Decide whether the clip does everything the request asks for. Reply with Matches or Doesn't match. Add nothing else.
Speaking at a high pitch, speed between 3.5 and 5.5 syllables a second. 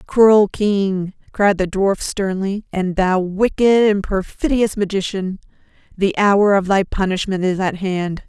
Matches